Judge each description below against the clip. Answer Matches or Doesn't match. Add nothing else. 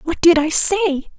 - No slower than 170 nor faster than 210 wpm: Matches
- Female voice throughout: Matches